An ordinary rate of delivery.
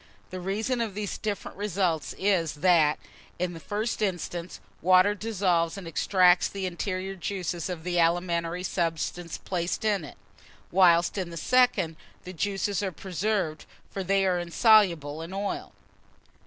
Yes: average, 145 wpm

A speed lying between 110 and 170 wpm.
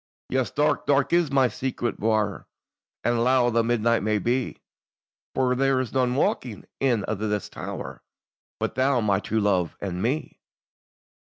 Yes: average, 155 wpm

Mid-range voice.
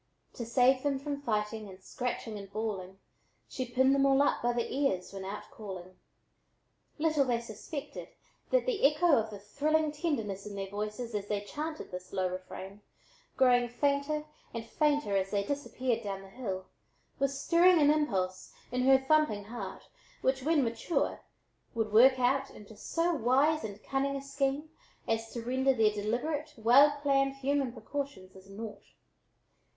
No: very high, 250 Hz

